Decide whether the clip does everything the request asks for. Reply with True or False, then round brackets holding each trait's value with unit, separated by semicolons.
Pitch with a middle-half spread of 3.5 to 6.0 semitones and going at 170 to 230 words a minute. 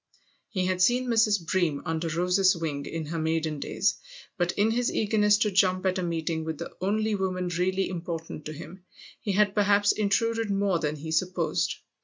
True (3.8 semitones; 185 wpm)